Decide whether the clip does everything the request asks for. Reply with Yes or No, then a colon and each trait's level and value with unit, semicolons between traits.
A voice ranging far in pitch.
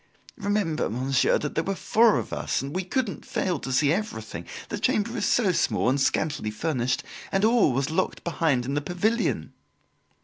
Yes: wide, 7.2 semitones